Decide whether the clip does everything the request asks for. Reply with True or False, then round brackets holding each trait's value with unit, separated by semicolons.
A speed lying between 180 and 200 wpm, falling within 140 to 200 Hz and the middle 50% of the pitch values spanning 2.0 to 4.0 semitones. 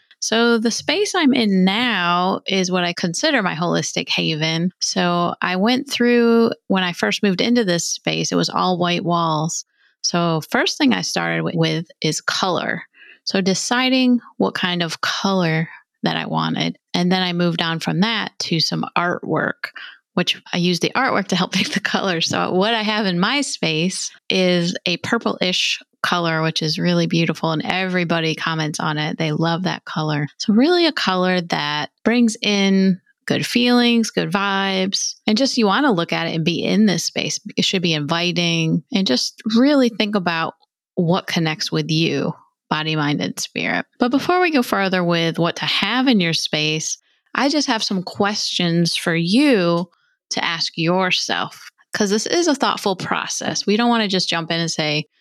False (185 wpm; 185 Hz; 5.4 semitones)